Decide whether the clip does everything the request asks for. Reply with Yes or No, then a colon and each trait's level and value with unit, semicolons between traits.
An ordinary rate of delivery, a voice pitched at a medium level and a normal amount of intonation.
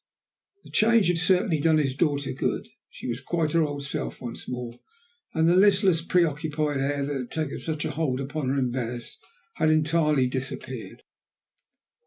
Yes: average, 170 wpm; medium, 150 Hz; average, 3.4 semitones